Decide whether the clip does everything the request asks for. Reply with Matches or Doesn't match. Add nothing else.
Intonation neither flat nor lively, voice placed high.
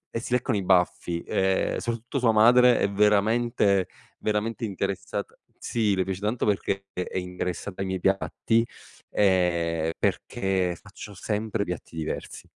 Doesn't match